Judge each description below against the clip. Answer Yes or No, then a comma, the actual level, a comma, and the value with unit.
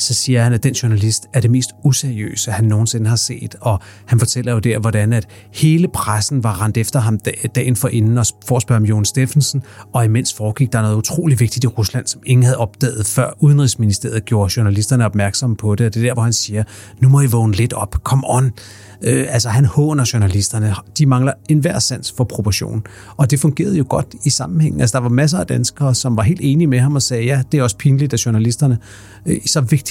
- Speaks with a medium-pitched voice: No, low, 120 Hz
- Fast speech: Yes, fast, 230 wpm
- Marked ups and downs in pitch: No, average, 3.4 semitones